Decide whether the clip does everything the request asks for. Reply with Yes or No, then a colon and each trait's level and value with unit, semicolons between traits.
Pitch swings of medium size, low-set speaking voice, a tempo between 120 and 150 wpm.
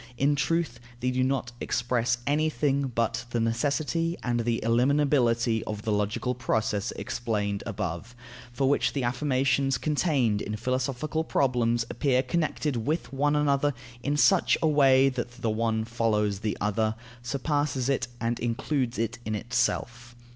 Yes: average, 3.5 semitones; low, 125 Hz; average, 145 wpm